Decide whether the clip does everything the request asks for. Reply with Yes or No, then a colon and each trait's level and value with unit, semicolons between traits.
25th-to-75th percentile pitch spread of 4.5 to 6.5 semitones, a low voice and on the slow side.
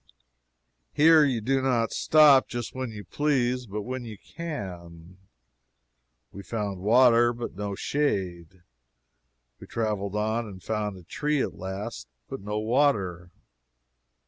Yes: average, 4.9 semitones; low, 110 Hz; slow, 130 wpm